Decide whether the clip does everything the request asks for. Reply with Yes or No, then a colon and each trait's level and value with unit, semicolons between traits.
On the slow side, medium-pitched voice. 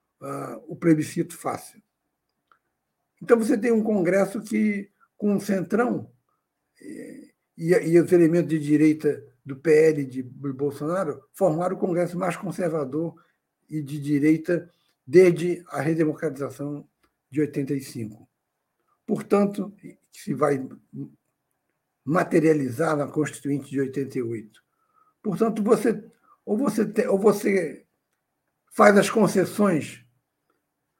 Yes: slow, 105 wpm; medium, 170 Hz